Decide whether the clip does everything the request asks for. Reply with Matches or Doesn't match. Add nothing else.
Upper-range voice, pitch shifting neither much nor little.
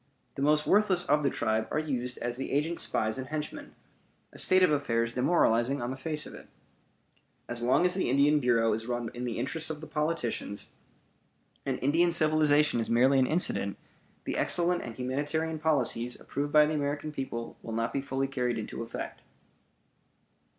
Doesn't match